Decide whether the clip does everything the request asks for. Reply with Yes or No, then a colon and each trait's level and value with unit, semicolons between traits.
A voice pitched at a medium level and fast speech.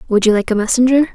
No: high, 235 Hz; fast, 260 wpm